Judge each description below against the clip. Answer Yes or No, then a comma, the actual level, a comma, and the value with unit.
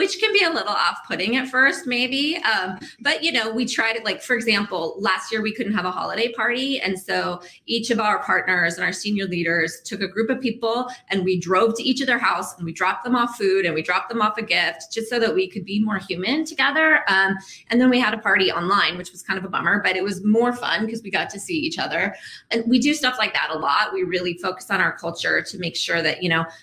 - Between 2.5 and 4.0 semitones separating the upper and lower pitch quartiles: No, average, 5.0 semitones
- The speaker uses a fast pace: Yes, fast, 265 wpm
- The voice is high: Yes, high, 215 Hz